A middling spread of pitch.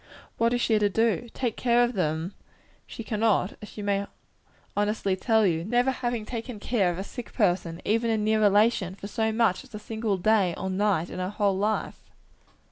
Yes: average, 3.0 semitones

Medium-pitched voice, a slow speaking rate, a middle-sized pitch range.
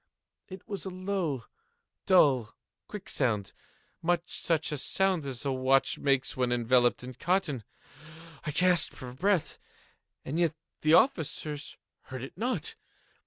No: medium, 150 Hz; slow, 125 wpm; wide, 5.8 semitones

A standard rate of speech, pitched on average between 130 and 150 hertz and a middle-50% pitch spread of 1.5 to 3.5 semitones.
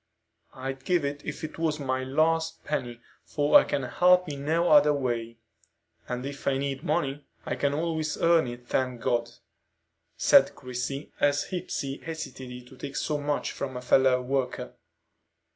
Yes: average, 160 wpm; medium, 140 Hz; average, 2.9 semitones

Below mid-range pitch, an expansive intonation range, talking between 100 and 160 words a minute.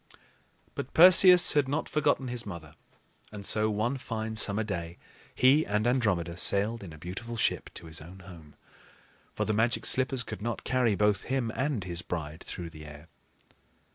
No: low, 110 Hz; wide, 6.0 semitones; average, 170 wpm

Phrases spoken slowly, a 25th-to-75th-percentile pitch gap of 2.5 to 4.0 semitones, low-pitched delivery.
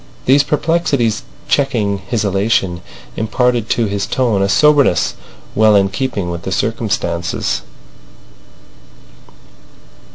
No: slow, 100 wpm; average, 4.6 semitones; low, 110 Hz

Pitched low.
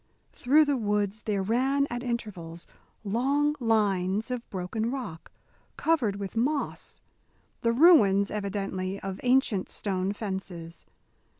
No: high, 210 Hz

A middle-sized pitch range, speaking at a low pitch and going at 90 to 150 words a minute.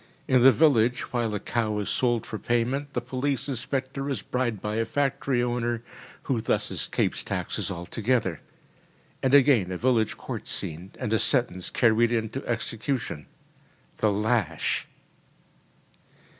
Yes: average, 3.1 semitones; low, 120 Hz; average, 140 wpm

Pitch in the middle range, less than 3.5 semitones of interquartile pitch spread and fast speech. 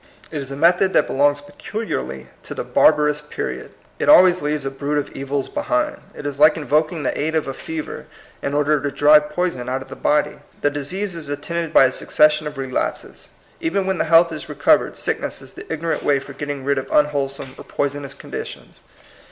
Yes: medium, 150 Hz; narrow, 2.5 semitones; fast, 210 wpm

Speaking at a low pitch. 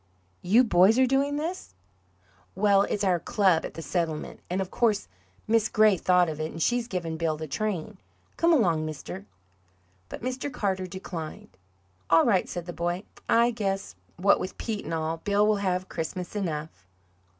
No: medium, 185 Hz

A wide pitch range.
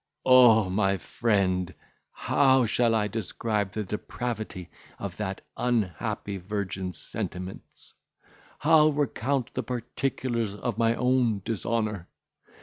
No: average, 3.9 semitones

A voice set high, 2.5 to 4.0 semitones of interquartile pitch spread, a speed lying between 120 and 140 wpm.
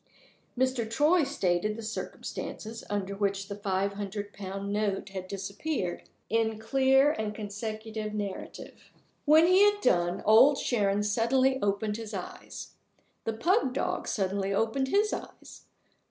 No: high, 215 Hz; average, 4.7 semitones; slow, 135 wpm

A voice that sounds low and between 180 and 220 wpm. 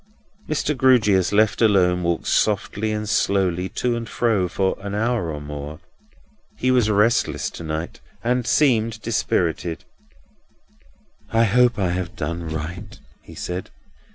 No: low, 100 Hz; slow, 135 wpm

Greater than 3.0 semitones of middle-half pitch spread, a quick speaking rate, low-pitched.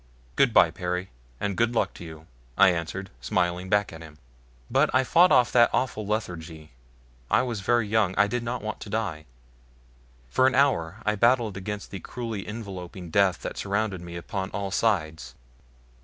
No: average, 4.5 semitones; average, 175 wpm; low, 100 Hz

